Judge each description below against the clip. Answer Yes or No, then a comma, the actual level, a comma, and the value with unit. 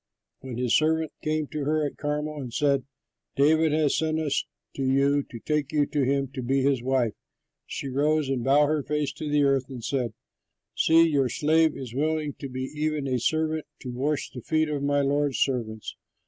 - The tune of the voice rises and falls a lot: No, narrow, 2.5 semitones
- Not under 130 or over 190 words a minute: No, average, 200 wpm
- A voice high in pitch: No, medium, 145 Hz